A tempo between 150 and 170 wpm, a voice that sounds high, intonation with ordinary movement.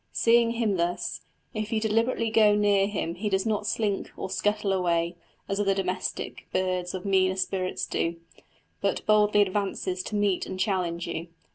No: average, 165 wpm; high, 195 Hz; narrow, 2.3 semitones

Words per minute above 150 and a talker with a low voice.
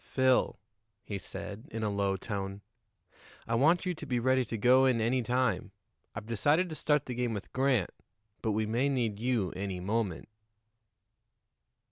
Yes: average, 165 wpm; low, 115 Hz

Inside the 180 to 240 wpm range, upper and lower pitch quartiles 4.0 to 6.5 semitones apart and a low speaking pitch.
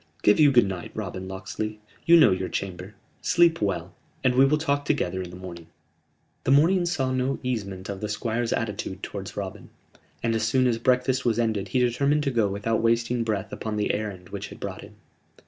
Yes: average, 200 wpm; average, 4.9 semitones; low, 115 Hz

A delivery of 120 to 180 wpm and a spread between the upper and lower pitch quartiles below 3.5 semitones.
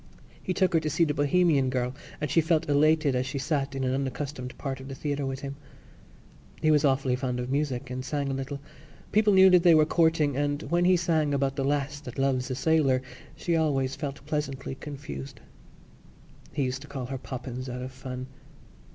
No: fast, 205 wpm; average, 2.7 semitones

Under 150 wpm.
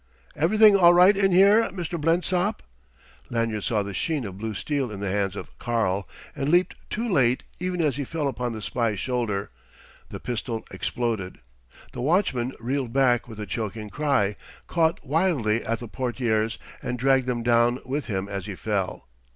No: average, 175 wpm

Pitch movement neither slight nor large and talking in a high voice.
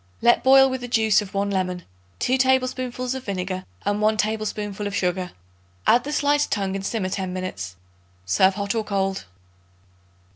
Yes: average, 4.6 semitones; high, 205 Hz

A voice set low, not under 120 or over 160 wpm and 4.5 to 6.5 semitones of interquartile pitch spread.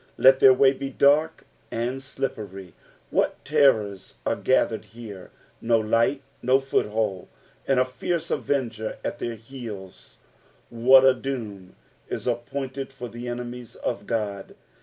No: low, 120 Hz; average, 140 wpm; average, 3.4 semitones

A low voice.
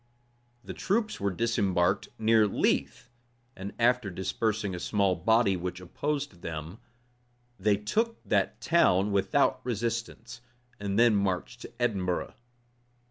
Yes: low, 105 Hz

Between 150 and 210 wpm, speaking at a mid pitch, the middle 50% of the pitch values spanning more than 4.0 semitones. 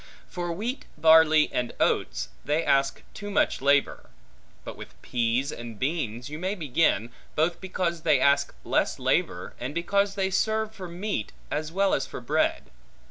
Yes: average, 160 wpm; medium, 160 Hz; wide, 5.5 semitones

